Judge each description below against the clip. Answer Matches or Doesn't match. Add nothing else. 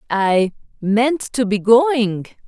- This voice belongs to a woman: Matches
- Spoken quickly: Doesn't match